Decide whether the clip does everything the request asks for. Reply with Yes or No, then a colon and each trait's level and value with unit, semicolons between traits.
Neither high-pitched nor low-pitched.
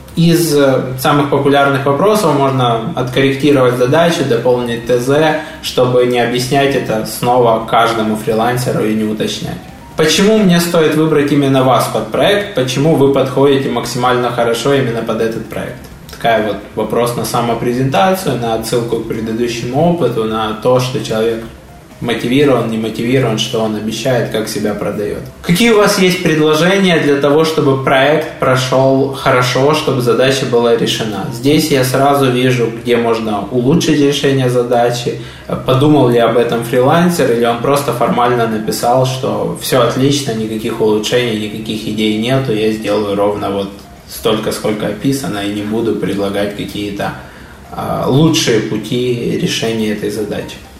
No: low, 125 Hz